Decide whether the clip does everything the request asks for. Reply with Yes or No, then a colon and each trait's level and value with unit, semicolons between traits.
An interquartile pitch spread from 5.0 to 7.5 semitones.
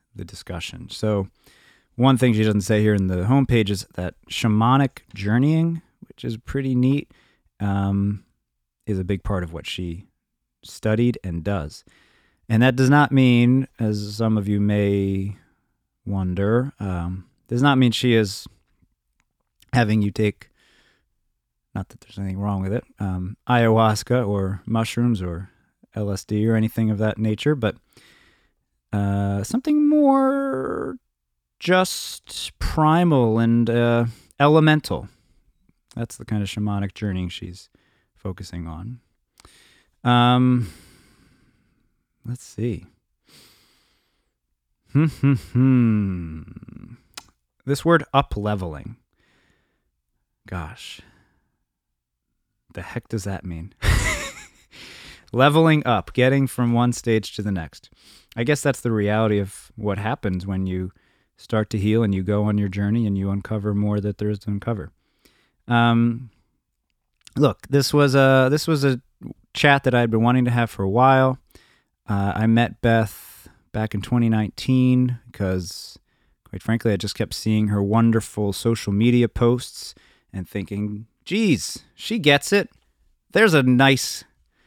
No: average, 4.1 semitones